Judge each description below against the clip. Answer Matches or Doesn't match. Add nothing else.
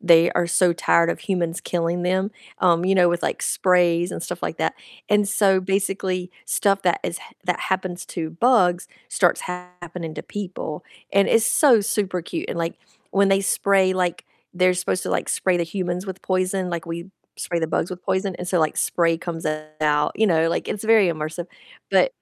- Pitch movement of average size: Doesn't match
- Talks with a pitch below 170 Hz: Doesn't match